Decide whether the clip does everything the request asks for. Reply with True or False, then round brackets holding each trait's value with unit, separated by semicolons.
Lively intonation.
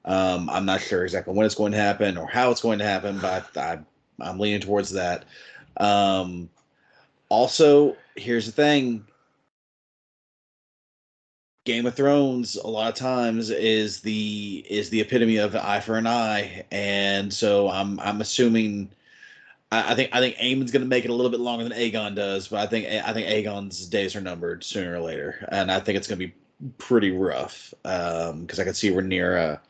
False (3.2 semitones)